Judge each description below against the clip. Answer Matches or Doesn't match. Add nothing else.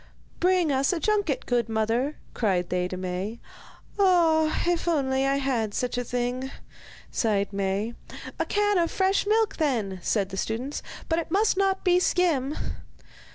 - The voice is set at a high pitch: Matches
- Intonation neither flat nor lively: Doesn't match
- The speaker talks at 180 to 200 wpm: Doesn't match